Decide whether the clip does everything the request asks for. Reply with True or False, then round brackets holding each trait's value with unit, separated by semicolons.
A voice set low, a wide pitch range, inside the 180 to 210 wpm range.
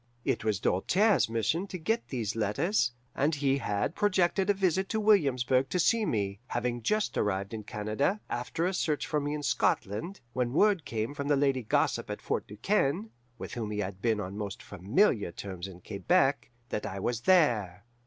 True (125 Hz; 8.8 semitones; 190 wpm)